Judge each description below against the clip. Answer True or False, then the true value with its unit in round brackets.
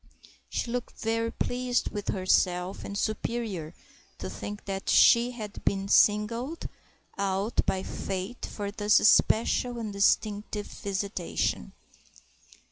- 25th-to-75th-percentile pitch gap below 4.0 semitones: True (2.9 semitones)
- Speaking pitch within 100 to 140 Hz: False (210 Hz)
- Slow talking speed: True (115 wpm)